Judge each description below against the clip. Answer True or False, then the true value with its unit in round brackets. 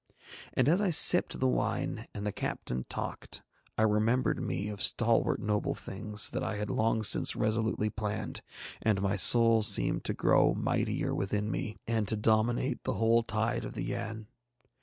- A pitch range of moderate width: False (1.6 semitones)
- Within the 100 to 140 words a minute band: False (170 wpm)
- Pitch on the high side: False (110 Hz)